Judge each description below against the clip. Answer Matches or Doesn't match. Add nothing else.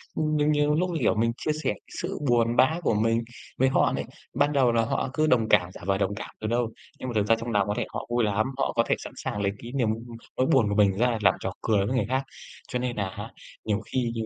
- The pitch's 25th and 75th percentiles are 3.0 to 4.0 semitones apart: Matches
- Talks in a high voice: Doesn't match